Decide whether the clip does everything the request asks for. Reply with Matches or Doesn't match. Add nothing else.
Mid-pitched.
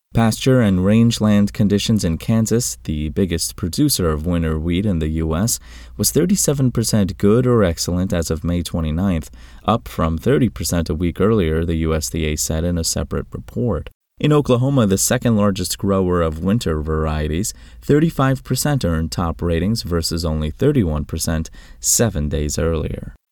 Doesn't match